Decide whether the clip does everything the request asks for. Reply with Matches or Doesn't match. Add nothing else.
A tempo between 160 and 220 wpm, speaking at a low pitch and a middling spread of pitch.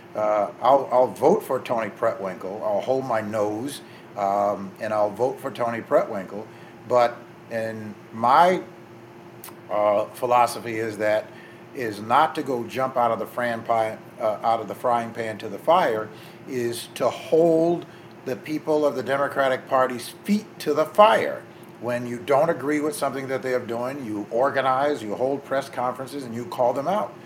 Matches